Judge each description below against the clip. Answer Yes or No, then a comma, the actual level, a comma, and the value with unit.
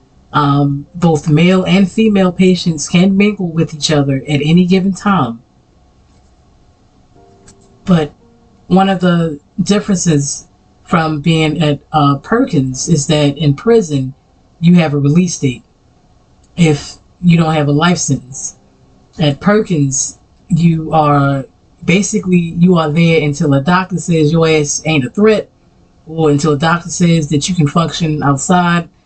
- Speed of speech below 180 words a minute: Yes, average, 140 wpm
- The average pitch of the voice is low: No, medium, 160 Hz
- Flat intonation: No, average, 3.8 semitones